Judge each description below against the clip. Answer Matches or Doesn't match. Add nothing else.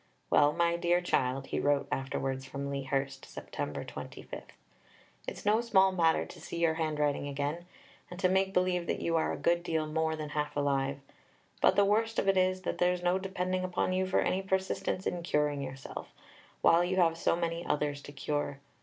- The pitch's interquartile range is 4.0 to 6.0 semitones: Matches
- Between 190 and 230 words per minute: Matches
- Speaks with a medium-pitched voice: Matches